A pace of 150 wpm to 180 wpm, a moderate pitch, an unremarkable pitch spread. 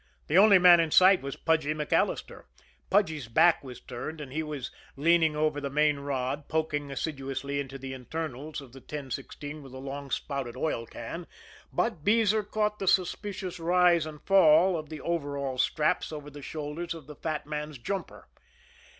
Yes: average, 170 wpm; medium, 150 Hz; average, 3.2 semitones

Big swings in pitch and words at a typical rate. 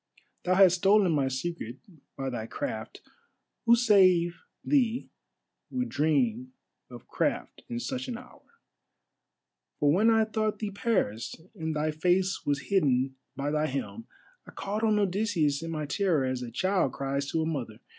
Yes: wide, 7.1 semitones; average, 155 wpm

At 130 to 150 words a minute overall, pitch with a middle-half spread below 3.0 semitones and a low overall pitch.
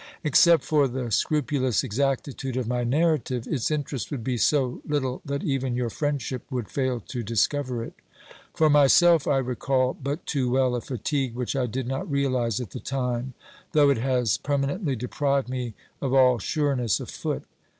No: average, 175 wpm; narrow, 2.4 semitones; low, 130 Hz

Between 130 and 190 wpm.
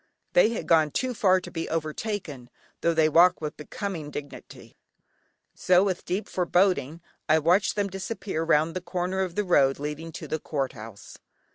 Yes: average, 170 wpm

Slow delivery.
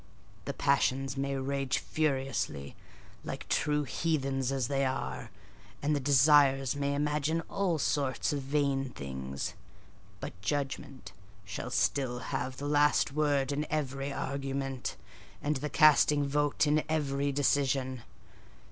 Yes: slow, 125 wpm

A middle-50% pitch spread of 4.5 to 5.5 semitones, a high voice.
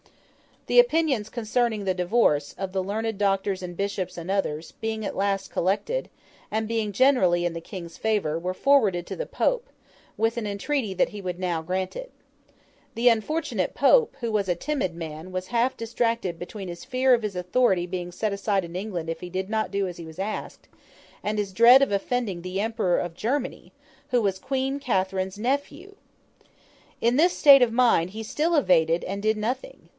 Yes: average, 4.8 semitones; high, 205 Hz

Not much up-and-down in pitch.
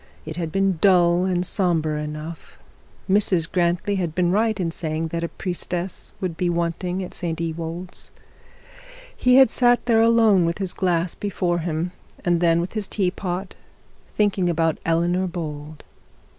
Yes: narrow, 2.3 semitones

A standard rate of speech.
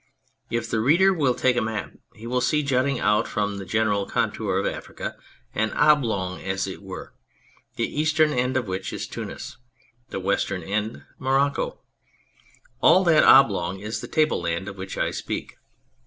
Yes: average, 165 wpm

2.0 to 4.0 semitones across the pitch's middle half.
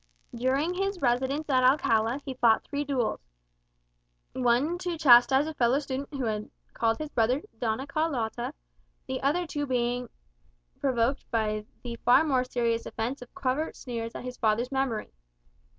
Yes: average, 3.1 semitones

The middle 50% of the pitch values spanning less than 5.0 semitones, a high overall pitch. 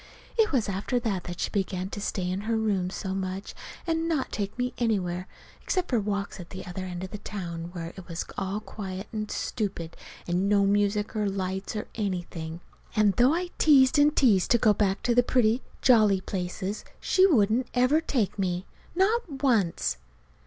Yes: average, 4.6 semitones; high, 205 Hz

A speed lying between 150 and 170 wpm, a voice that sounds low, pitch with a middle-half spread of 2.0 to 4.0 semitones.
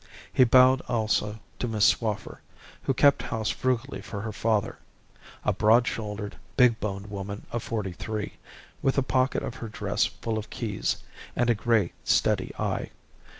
Yes: average, 160 wpm; low, 110 Hz; average, 2.8 semitones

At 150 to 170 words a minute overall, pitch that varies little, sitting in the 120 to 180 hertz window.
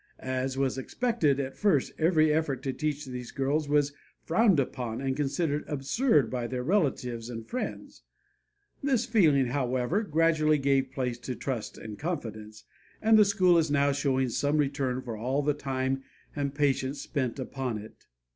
No: average, 160 wpm; average, 3.1 semitones; medium, 140 Hz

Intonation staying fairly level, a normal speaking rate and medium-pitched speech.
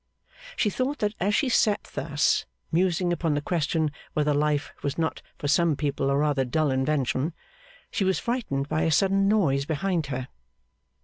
No: average, 4.9 semitones; average, 170 wpm; medium, 155 Hz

